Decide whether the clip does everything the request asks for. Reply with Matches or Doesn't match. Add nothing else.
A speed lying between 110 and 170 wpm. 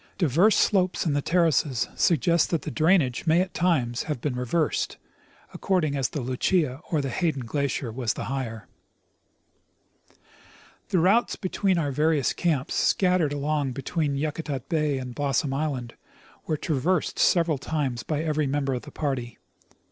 Matches